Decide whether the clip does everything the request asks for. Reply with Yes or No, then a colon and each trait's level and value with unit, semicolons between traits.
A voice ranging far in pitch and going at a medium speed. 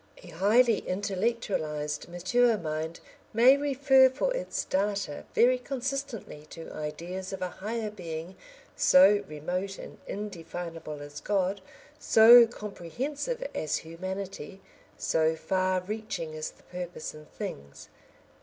No: wide, 5.9 semitones; slow, 115 wpm